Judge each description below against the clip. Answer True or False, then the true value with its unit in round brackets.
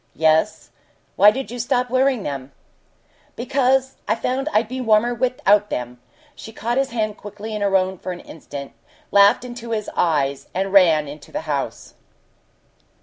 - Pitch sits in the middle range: False (210 Hz)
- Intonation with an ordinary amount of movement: False (6.5 semitones)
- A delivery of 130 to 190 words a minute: True (160 wpm)